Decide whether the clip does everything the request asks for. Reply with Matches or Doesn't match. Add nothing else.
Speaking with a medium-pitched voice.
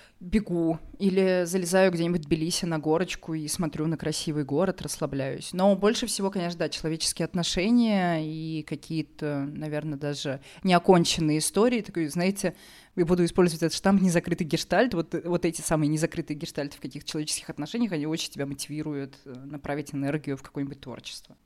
Matches